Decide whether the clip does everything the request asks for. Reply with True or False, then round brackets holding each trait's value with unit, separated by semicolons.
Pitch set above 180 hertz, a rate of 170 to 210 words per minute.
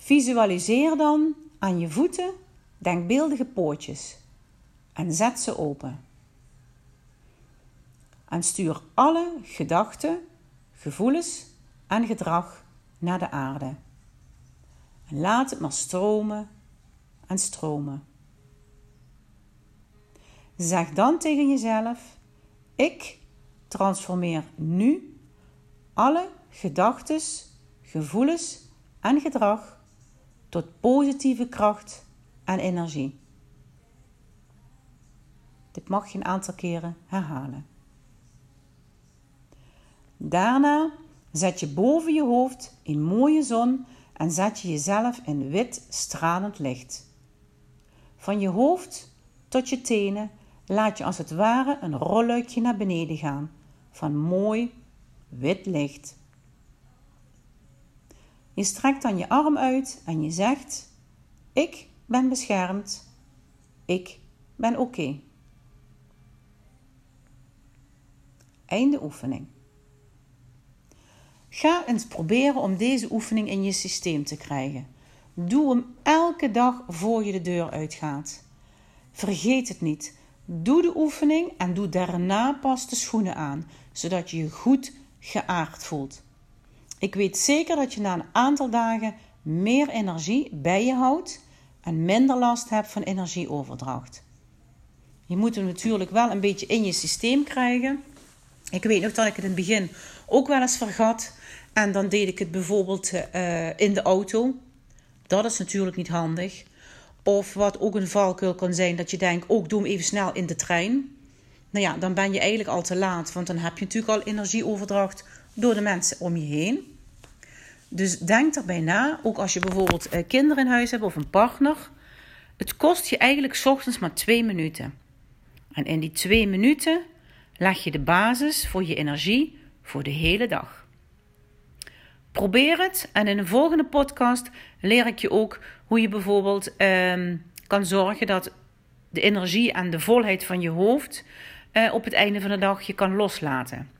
False (190 Hz; 135 wpm)